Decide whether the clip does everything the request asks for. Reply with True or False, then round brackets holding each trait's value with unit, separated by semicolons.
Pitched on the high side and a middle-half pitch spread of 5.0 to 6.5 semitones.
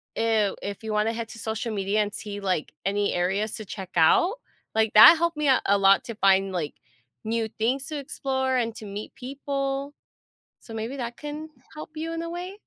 True (225 Hz; 5.3 semitones)